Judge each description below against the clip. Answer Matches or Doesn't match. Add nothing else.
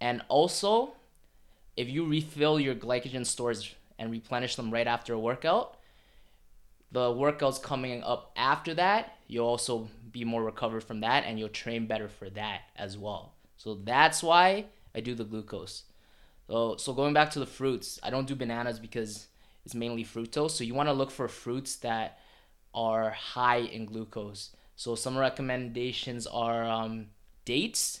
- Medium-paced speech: Matches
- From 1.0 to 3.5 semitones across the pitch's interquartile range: Matches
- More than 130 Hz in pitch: Doesn't match